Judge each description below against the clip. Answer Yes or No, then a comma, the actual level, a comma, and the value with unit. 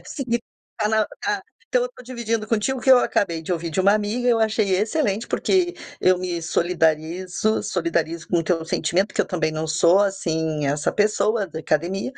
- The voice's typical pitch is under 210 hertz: Yes, high, 190 Hz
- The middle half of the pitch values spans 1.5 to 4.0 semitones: No, average, 4.9 semitones